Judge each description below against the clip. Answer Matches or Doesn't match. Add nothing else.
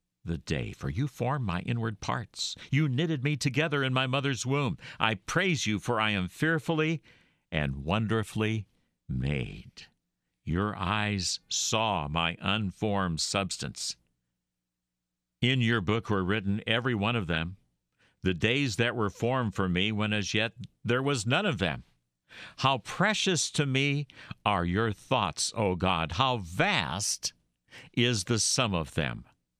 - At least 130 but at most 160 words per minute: Matches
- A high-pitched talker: Doesn't match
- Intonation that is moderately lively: Doesn't match